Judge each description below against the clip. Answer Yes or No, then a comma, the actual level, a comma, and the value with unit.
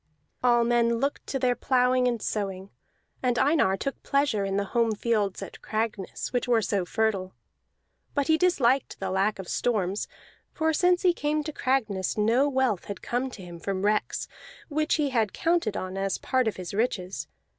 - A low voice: No, high, 235 Hz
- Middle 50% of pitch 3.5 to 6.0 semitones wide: Yes, average, 5.1 semitones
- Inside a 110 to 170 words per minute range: No, average, 180 wpm